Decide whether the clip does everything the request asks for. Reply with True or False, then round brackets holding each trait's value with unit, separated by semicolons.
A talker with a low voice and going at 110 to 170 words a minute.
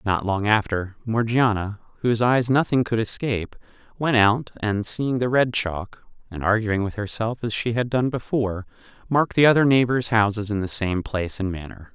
False (110 Hz; 180 wpm)